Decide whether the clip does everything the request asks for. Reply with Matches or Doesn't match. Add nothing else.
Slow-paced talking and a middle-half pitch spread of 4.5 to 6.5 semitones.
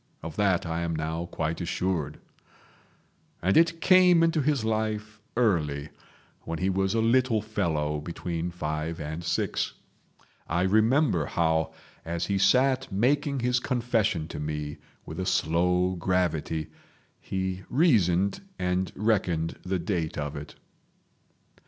Matches